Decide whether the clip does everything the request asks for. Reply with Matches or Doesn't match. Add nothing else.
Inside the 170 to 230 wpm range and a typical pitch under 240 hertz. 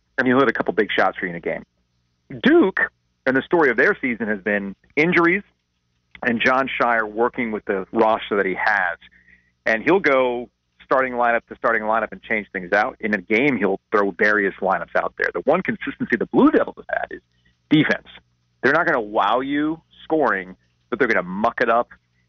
Matches